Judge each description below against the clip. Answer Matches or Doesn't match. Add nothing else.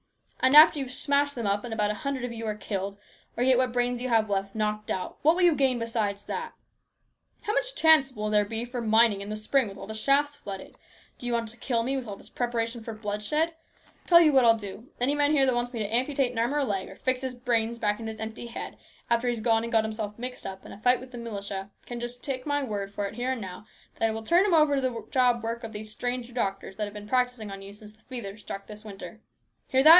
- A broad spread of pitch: Doesn't match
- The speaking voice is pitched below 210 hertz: Doesn't match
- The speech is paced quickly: Matches